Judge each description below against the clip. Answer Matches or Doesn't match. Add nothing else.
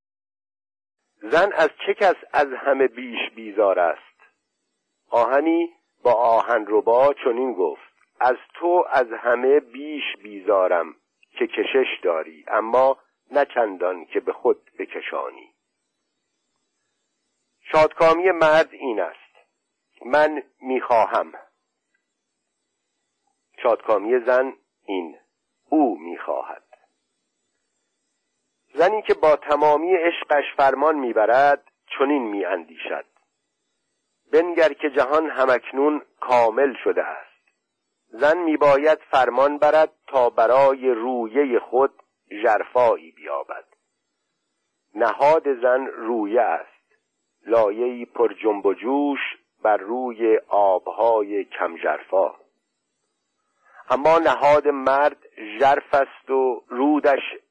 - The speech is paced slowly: Matches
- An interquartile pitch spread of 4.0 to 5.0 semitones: Matches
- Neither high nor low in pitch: Matches